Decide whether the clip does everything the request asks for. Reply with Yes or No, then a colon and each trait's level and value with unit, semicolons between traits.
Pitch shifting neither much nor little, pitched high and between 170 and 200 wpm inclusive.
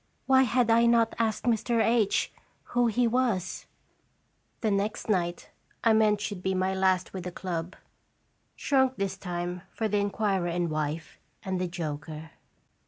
No: average, 4.2 semitones; high, 195 Hz; average, 155 wpm